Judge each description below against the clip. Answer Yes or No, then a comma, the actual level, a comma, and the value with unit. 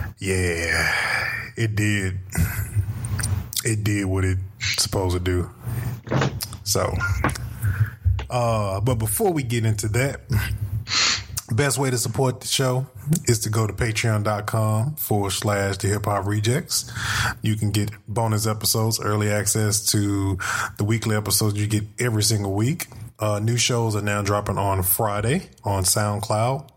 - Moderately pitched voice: No, low, 105 Hz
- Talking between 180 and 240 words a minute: No, slow, 135 wpm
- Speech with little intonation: Yes, narrow, 2.2 semitones